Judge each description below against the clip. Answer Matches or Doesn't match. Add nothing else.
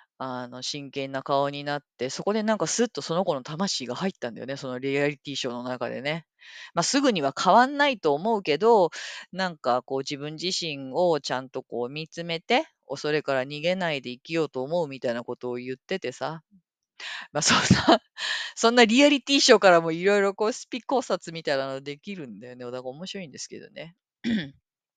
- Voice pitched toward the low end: Doesn't match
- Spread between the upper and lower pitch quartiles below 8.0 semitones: Matches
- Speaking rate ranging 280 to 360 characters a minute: Doesn't match